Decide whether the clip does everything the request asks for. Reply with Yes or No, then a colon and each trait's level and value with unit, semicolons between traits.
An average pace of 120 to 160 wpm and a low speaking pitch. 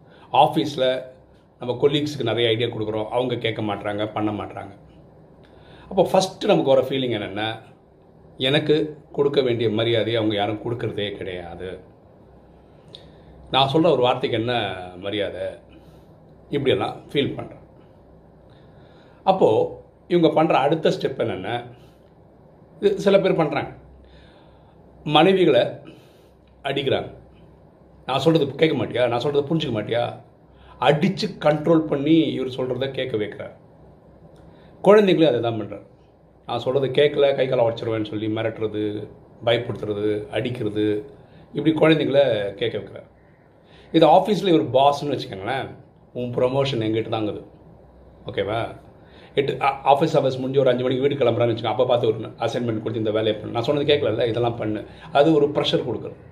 Yes: average, 125 wpm; low, 130 Hz